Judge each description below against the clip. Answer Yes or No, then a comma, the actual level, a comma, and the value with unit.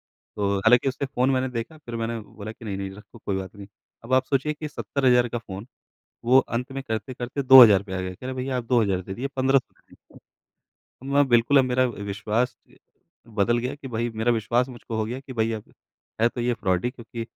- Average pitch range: Yes, average, 3.1 semitones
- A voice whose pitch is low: Yes, low, 120 Hz